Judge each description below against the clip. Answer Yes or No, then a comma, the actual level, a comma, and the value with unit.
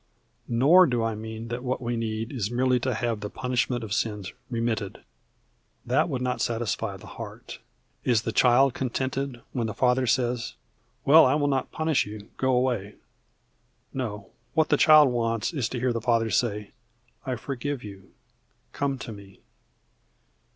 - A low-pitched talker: Yes, low, 120 Hz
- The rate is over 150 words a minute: Yes, average, 165 wpm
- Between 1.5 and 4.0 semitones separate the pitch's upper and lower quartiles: Yes, average, 2.7 semitones